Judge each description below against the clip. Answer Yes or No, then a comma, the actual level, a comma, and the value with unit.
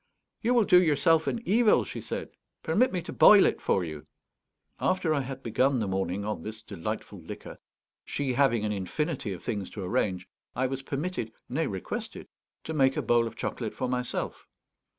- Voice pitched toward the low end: Yes, low, 130 Hz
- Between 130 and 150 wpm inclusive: No, average, 185 wpm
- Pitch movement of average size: No, wide, 7.2 semitones